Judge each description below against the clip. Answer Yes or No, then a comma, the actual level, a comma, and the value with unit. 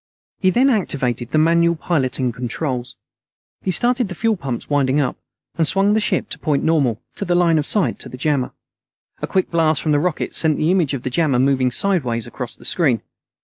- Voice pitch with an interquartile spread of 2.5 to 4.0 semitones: No, wide, 5.5 semitones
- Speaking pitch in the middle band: Yes, medium, 155 Hz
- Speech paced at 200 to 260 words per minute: Yes, fast, 205 wpm